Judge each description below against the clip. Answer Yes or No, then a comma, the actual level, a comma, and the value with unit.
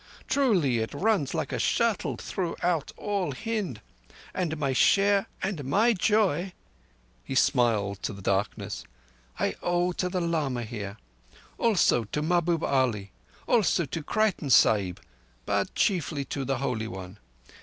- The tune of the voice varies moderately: No, wide, 9.0 semitones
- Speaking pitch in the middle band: Yes, medium, 145 Hz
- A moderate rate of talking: No, slow, 125 wpm